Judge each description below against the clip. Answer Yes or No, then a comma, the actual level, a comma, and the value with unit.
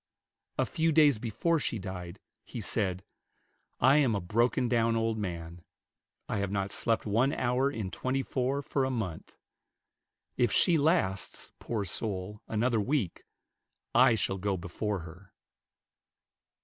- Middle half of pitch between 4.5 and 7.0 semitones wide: Yes, average, 5.0 semitones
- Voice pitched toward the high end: No, low, 110 Hz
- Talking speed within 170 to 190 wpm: No, average, 140 wpm